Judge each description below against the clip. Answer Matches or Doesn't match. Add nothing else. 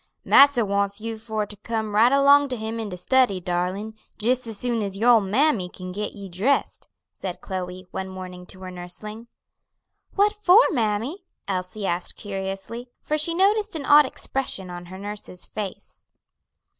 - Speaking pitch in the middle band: Doesn't match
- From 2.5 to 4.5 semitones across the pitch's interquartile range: Doesn't match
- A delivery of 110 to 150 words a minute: Doesn't match